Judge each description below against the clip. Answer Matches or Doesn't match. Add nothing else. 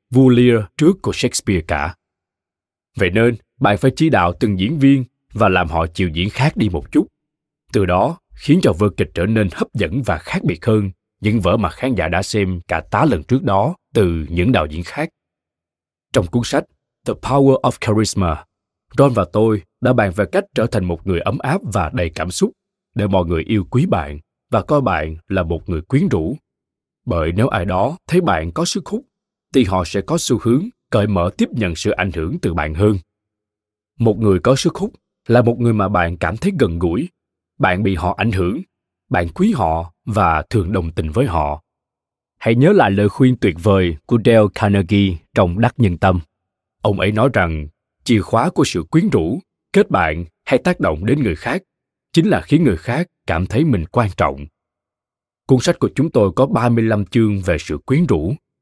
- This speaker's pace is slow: Doesn't match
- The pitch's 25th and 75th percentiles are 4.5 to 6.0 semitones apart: Matches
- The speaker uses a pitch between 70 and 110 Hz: Matches